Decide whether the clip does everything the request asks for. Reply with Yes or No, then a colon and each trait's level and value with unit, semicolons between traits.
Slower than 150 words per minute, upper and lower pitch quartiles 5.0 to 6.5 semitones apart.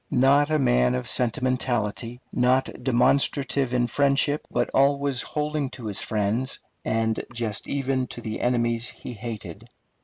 No: average, 140 wpm; average, 3.3 semitones